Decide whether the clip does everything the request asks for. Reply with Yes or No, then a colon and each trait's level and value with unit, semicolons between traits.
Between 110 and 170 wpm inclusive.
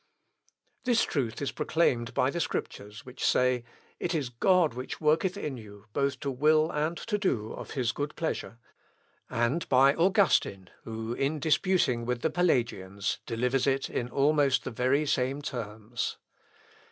Yes: average, 155 wpm